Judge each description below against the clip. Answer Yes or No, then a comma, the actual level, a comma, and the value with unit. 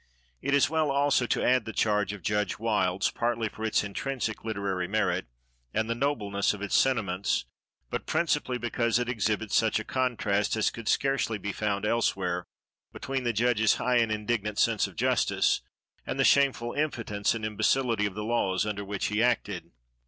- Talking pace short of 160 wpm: No, average, 175 wpm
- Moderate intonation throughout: Yes, average, 3.0 semitones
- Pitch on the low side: Yes, low, 110 Hz